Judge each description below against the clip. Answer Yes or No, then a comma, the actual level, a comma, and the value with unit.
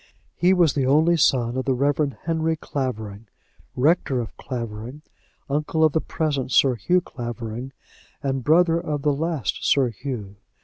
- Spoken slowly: No, average, 150 wpm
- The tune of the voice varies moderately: Yes, average, 4.5 semitones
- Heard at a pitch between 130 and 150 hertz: Yes, medium, 140 Hz